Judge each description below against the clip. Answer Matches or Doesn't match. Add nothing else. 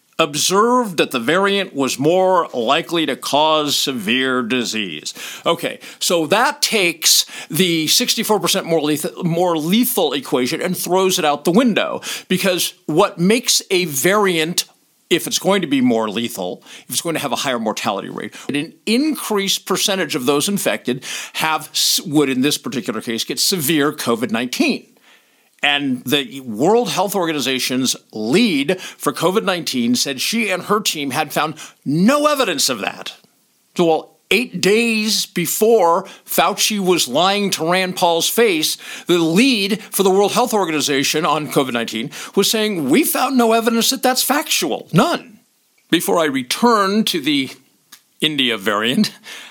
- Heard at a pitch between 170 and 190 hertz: Matches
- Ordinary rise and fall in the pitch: Doesn't match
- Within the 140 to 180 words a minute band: Matches